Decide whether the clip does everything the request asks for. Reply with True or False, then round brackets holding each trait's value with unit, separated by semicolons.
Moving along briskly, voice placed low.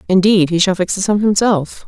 False (225 wpm; 190 Hz)